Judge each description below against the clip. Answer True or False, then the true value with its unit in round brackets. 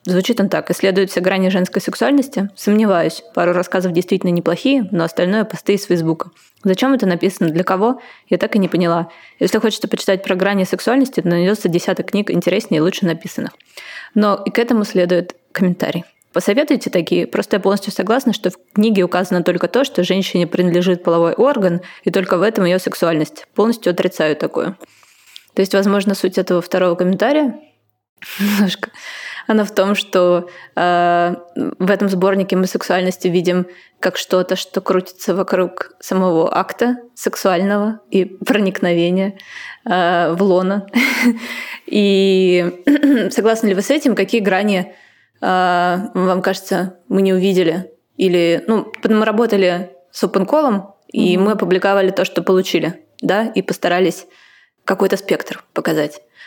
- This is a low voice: False (190 Hz)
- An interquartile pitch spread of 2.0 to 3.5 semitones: True (2.6 semitones)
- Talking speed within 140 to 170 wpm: True (145 wpm)